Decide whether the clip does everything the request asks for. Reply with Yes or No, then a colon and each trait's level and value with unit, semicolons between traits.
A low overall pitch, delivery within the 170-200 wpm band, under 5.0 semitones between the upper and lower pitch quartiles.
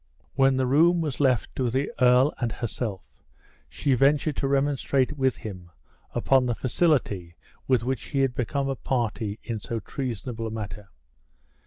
No: low, 125 Hz; average, 160 wpm; average, 3.2 semitones